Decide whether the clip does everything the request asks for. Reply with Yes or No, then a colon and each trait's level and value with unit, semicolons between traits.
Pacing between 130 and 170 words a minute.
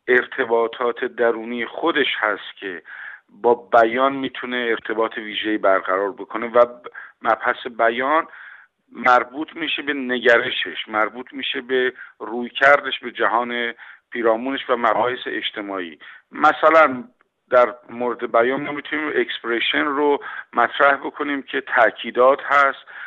No: average, 110 wpm